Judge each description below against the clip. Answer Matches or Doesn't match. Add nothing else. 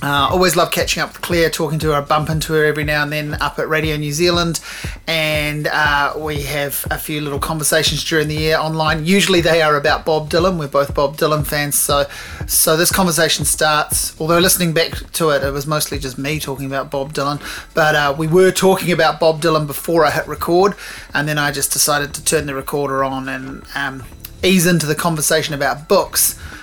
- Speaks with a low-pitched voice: Doesn't match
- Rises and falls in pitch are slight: Matches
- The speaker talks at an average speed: Doesn't match